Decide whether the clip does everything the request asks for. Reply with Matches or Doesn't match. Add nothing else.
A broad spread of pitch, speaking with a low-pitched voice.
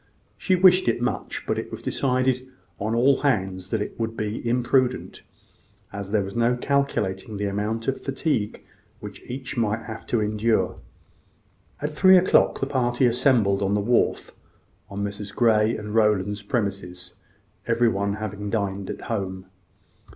Doesn't match